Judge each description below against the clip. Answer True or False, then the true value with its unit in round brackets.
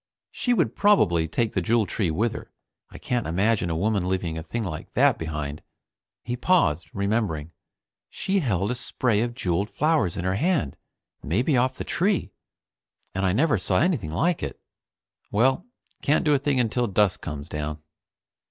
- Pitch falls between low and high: False (105 Hz)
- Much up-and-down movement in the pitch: True (7.3 semitones)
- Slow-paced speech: False (170 wpm)